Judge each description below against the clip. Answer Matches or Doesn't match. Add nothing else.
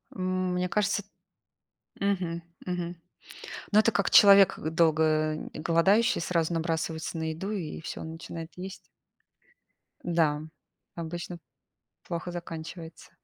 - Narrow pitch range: Matches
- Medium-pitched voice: Matches